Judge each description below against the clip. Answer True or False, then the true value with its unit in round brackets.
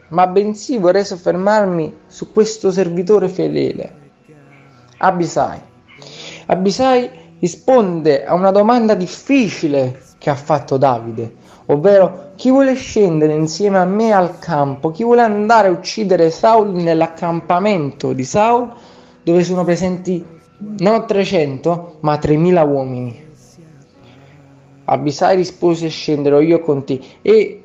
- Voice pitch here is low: False (175 Hz)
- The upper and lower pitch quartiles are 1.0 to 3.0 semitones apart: False (5.0 semitones)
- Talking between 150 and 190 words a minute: False (115 wpm)